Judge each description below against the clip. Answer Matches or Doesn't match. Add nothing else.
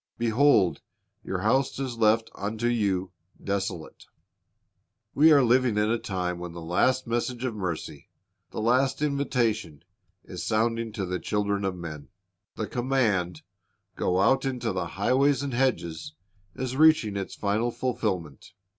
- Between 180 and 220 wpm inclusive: Doesn't match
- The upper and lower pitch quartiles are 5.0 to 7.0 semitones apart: Matches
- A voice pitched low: Matches